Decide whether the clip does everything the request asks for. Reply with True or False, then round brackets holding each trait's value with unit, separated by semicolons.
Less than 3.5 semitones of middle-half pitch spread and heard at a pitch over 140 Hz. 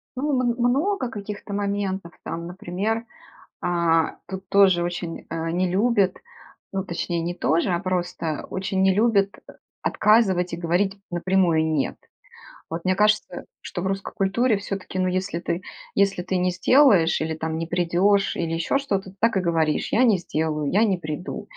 True (2.9 semitones; 185 Hz)